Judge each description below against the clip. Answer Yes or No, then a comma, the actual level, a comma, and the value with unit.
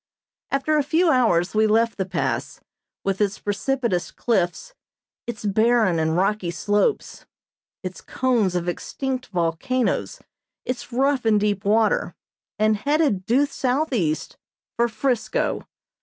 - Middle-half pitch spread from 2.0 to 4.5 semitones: No, average, 5.2 semitones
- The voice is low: No, high, 220 Hz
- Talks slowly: Yes, slow, 125 wpm